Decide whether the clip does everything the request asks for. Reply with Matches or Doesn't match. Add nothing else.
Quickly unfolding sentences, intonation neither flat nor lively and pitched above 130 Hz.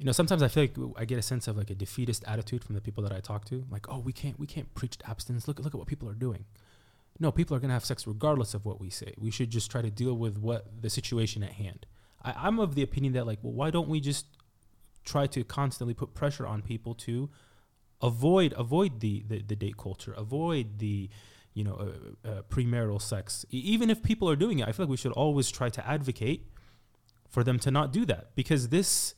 Doesn't match